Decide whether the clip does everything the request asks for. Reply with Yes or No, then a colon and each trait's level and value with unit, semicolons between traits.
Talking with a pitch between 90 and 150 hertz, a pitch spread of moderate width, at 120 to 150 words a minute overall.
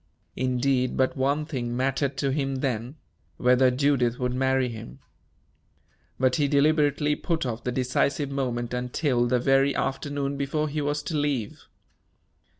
No: low, 135 Hz; narrow, 2.3 semitones; average, 145 wpm